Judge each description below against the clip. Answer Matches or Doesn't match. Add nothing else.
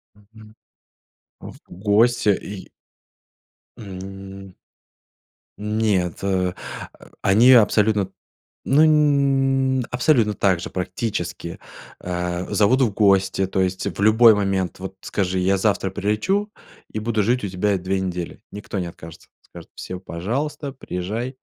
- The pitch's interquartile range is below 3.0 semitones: Doesn't match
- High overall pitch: Doesn't match